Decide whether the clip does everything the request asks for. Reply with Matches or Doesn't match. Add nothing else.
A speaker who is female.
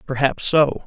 Doesn't match